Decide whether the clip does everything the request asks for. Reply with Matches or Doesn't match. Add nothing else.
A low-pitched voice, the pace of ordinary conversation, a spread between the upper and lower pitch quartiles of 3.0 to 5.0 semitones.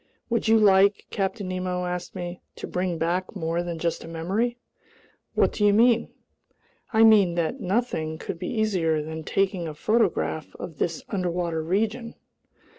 Doesn't match